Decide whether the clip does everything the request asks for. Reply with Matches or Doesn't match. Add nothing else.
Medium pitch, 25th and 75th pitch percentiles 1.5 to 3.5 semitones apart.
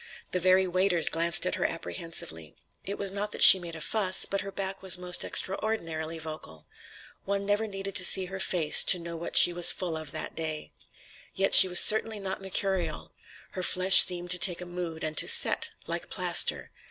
Matches